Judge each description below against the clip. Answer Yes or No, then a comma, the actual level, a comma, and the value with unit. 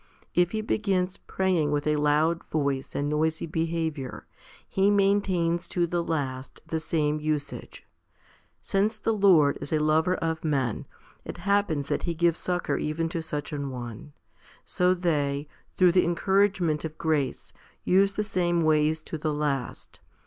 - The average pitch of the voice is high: No, medium, 160 Hz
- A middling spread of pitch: Yes, average, 3.4 semitones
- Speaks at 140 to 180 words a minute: Yes, average, 155 wpm